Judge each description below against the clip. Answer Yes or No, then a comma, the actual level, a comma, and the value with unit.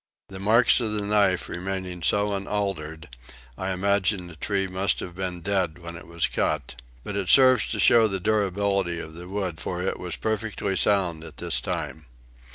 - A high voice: No, very low, 95 Hz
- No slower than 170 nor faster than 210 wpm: Yes, average, 180 wpm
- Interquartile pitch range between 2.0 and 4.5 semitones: Yes, average, 2.8 semitones